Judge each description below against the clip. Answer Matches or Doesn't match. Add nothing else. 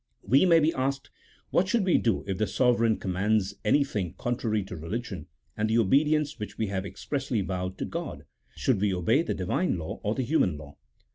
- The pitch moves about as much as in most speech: Doesn't match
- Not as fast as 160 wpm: Doesn't match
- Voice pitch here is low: Matches